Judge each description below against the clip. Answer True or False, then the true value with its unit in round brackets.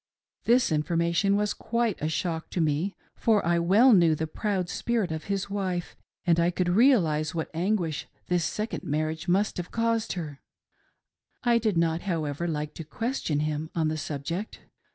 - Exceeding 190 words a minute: False (170 wpm)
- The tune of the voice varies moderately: True (4.5 semitones)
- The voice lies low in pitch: False (175 Hz)